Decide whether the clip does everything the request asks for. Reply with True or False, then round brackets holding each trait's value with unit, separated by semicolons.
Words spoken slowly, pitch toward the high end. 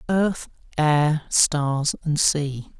False (110 wpm; 150 Hz)